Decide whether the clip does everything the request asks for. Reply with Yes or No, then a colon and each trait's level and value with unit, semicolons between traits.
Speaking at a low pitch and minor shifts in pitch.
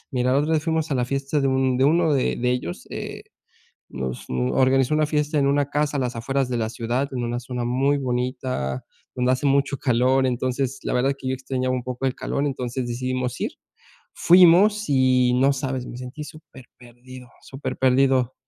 Yes: low, 130 Hz; narrow, 1.8 semitones